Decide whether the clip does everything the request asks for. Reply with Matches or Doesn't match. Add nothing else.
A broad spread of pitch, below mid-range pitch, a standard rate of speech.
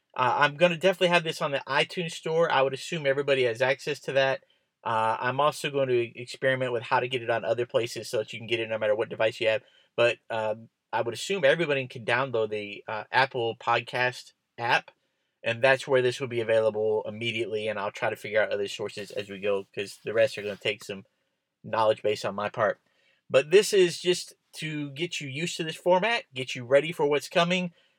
Doesn't match